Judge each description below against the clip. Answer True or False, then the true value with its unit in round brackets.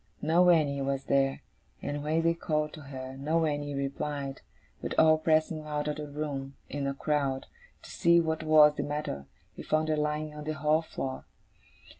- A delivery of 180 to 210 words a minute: True (185 wpm)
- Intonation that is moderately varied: False (2.1 semitones)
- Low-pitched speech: False (150 Hz)